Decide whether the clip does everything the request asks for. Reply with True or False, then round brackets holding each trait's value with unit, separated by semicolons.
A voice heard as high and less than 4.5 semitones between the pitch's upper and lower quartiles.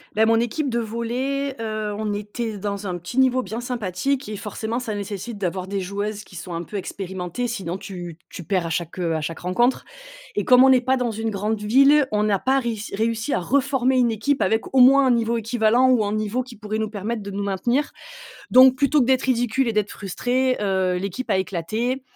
True (220 Hz; 4.1 semitones)